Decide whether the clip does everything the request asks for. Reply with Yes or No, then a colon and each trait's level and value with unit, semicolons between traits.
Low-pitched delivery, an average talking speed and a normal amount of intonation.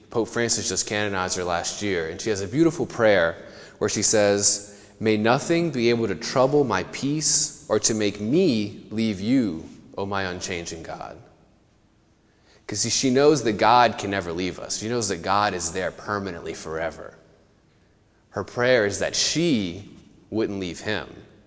Yes: low, 105 Hz; average, 165 wpm; average, 3.1 semitones